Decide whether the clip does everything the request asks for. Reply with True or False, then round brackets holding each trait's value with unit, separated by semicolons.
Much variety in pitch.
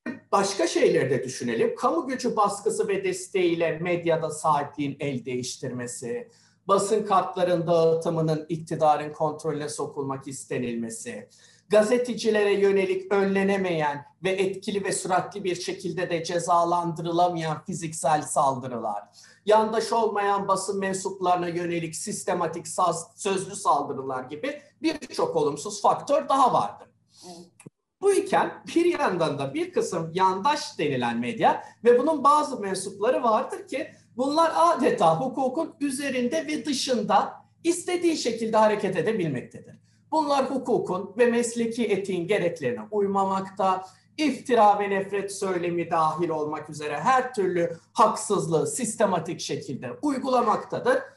True (6.6 semitones)